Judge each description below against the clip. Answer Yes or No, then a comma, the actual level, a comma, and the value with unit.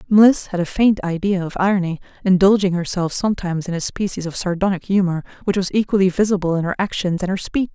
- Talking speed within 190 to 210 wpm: Yes, average, 200 wpm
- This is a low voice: No, medium, 185 Hz